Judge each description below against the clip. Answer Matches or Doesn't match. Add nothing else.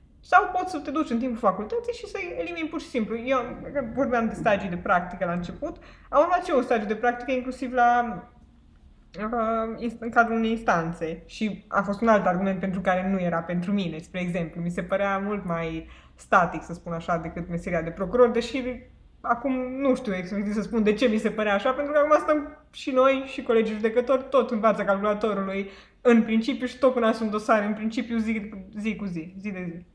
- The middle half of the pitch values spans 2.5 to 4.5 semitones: Doesn't match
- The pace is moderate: Doesn't match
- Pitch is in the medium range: Doesn't match